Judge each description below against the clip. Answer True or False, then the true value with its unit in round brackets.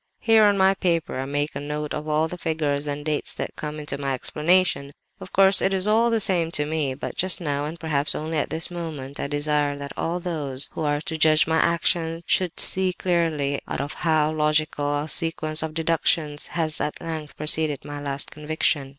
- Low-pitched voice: False (155 Hz)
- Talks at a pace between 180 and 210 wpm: True (205 wpm)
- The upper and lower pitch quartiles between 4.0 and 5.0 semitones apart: False (2.4 semitones)